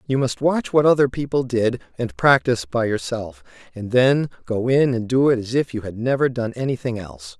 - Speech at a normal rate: No, fast, 210 wpm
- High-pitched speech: No, low, 120 Hz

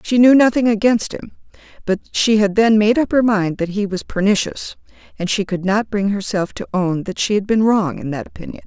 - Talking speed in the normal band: No, fast, 230 wpm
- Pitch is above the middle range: Yes, high, 205 Hz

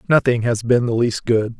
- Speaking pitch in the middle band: No, low, 120 Hz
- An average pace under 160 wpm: No, fast, 225 wpm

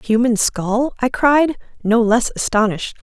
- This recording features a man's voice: No, female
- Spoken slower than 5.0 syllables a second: Yes, 4.6 syllables/s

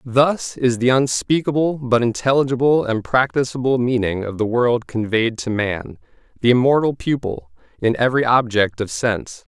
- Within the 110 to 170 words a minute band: Yes, average, 145 wpm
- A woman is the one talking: No, male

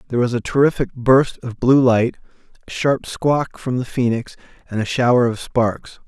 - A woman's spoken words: No, male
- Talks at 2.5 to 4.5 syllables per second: No, 4.8 syllables/s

